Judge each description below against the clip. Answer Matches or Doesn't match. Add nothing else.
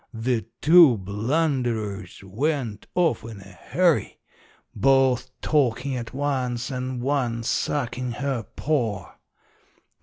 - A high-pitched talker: Doesn't match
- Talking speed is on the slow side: Matches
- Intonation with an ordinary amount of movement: Matches